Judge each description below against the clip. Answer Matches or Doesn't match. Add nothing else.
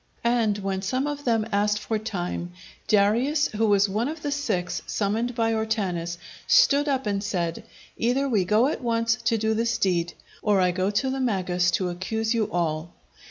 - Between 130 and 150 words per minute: Doesn't match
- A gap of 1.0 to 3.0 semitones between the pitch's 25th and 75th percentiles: Doesn't match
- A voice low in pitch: Doesn't match